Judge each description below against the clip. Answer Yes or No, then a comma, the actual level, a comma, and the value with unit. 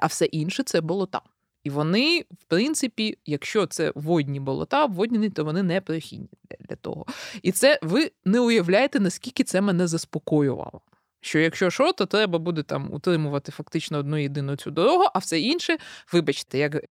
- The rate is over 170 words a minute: No, average, 165 wpm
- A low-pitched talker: No, medium, 175 Hz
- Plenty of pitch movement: Yes, wide, 5.9 semitones